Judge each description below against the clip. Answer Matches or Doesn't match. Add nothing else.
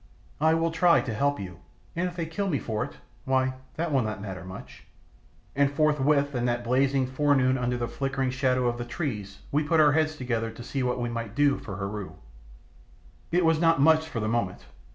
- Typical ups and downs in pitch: Matches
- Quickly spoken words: Matches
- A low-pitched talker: Matches